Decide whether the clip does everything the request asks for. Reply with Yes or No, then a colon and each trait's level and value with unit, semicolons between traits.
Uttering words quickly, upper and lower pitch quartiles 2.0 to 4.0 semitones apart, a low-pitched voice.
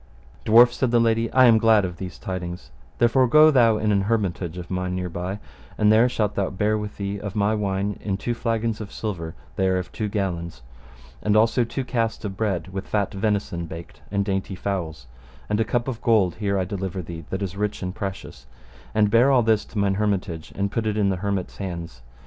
Yes: fast, 215 wpm; average, 3.1 semitones; low, 100 Hz